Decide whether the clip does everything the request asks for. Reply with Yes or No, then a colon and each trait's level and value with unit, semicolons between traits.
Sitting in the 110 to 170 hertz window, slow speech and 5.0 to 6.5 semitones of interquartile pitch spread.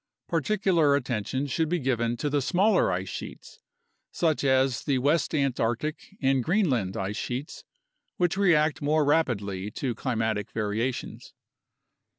Yes: low, 135 Hz; slow, 130 wpm; average, 5.3 semitones